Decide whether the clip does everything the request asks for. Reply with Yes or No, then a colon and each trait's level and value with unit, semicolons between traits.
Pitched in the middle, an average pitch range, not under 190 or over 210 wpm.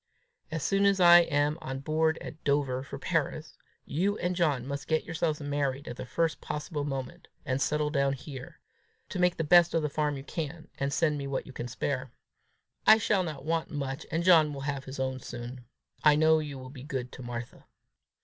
Yes: medium, 145 Hz; average, 3.2 semitones; fast, 205 wpm